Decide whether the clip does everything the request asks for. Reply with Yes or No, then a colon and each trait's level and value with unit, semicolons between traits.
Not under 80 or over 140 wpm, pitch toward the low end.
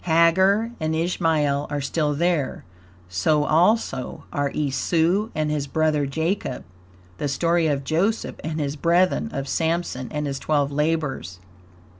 No: slow, 135 wpm; medium, 155 Hz